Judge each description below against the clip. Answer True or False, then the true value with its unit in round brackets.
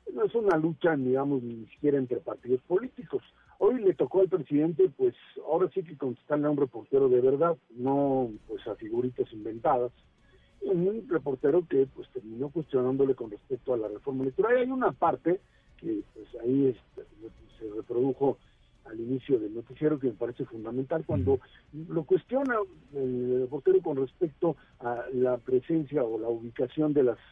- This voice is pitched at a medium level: True (150 Hz)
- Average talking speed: True (165 wpm)